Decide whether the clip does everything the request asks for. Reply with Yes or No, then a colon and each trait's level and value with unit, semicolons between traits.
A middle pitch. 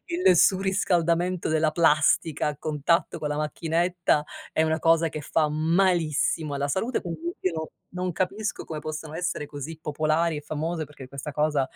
Yes: medium, 160 Hz